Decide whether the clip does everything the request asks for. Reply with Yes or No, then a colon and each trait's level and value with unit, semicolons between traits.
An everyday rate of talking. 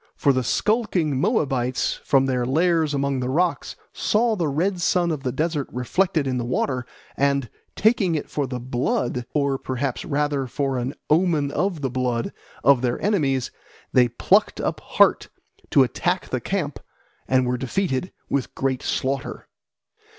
Yes: average, 160 wpm